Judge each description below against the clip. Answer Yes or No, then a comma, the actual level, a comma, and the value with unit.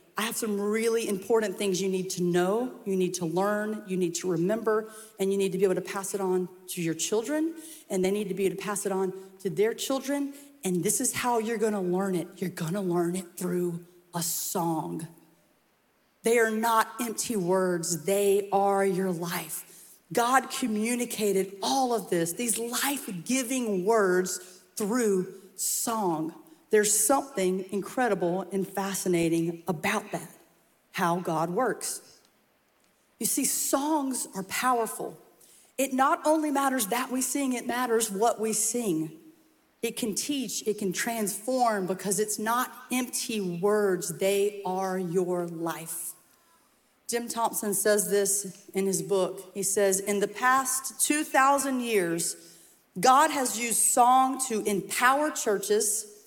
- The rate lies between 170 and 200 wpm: No, average, 150 wpm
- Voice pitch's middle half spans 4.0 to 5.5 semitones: Yes, average, 4.3 semitones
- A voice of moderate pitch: No, high, 205 Hz